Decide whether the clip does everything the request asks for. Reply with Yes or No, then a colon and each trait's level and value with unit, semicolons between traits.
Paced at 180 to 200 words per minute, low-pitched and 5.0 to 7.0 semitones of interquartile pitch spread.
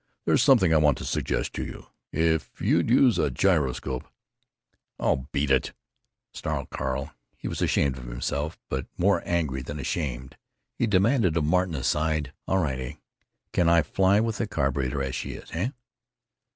No: average, 165 wpm; very low, 75 Hz; wide, 5.6 semitones